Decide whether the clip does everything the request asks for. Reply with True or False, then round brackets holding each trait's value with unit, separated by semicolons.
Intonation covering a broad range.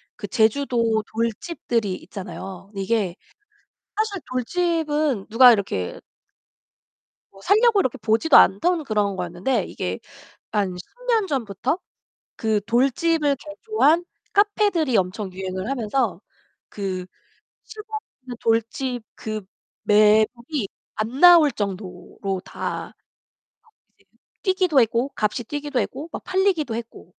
True (7.0 semitones)